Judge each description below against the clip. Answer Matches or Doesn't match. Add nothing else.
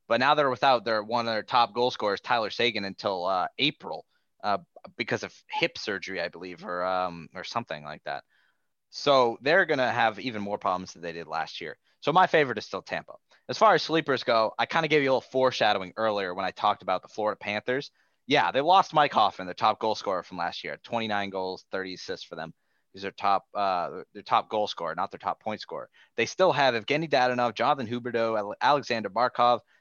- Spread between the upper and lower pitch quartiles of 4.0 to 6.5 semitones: Matches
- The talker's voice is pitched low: Matches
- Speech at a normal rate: Doesn't match